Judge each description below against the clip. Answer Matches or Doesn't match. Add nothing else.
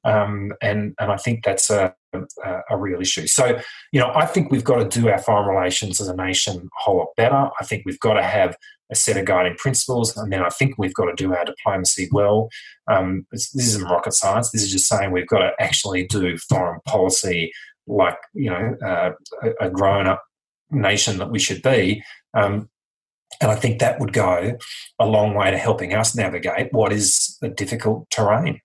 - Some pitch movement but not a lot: Matches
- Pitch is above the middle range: Doesn't match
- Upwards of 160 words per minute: Matches